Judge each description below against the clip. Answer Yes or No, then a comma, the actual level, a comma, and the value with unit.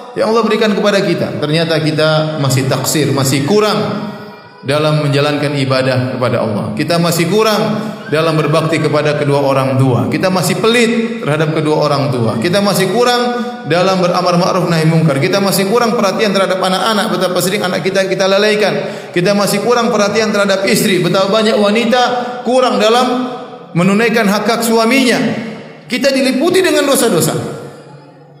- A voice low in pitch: No, high, 195 Hz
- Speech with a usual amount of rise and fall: No, wide, 6.1 semitones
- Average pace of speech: No, fast, 145 wpm